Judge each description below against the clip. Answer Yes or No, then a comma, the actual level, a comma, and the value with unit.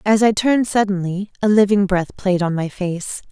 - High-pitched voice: Yes, high, 195 Hz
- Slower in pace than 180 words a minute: No, average, 200 wpm